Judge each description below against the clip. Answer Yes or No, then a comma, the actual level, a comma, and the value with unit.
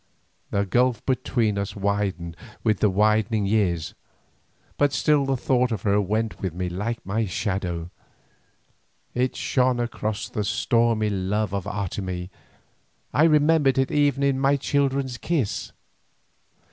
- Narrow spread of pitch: No, average, 4.9 semitones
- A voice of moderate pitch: No, low, 110 Hz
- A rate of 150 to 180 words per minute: No, slow, 135 wpm